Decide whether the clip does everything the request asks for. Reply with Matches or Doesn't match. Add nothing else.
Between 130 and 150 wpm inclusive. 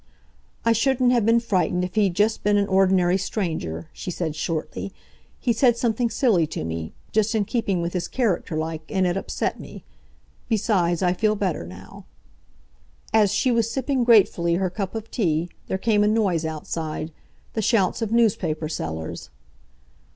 Doesn't match